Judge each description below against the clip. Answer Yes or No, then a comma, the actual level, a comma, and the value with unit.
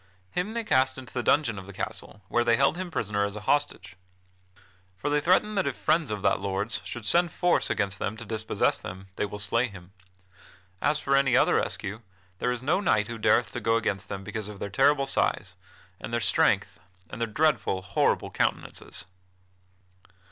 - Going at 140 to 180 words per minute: No, average, 195 wpm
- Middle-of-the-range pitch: No, low, 115 Hz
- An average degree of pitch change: No, wide, 6.1 semitones